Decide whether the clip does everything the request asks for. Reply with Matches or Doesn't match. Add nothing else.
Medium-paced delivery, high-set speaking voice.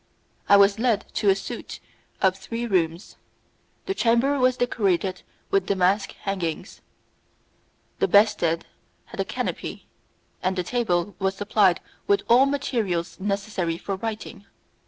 Doesn't match